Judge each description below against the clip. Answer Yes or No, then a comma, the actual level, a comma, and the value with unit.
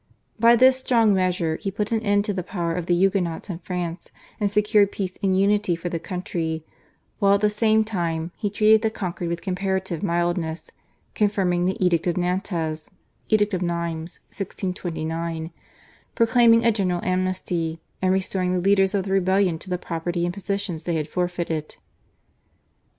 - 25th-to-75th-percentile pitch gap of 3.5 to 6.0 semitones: No, average, 3.0 semitones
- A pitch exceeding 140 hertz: Yes, medium, 185 Hz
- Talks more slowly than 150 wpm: No, average, 165 wpm